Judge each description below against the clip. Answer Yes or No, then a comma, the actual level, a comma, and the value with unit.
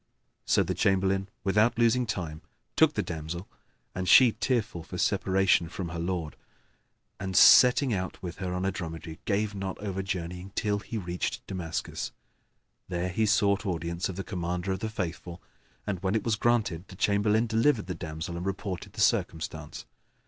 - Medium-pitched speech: No, very low, 95 Hz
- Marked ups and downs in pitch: No, average, 3.3 semitones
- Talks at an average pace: Yes, average, 170 wpm